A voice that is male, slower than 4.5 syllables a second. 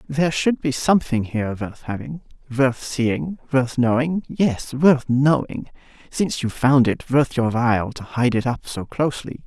No: male; 4.6 syllables/s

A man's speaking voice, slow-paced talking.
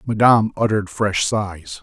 Yes: male; slow, 130 wpm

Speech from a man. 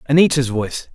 Yes: male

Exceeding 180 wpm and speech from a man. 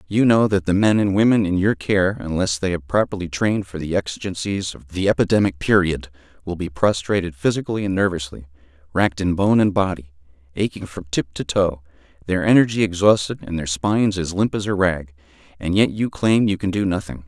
Yes: average, 200 wpm; male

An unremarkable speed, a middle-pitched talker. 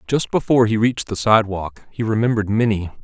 No: average, 180 wpm; low, 110 Hz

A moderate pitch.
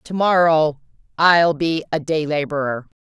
Yes: medium, 155 Hz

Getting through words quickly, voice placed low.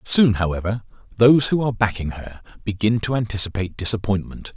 No: average, 145 wpm; low, 105 Hz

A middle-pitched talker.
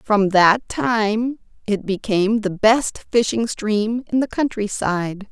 No: high, 210 Hz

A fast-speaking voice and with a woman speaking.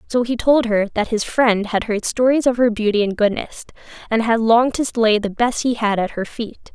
Yes: fast, 240 wpm; female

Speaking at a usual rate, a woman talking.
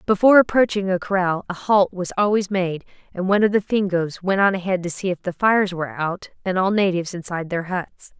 No: fast, 220 wpm; female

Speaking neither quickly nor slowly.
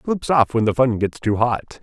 No: fast, 265 wpm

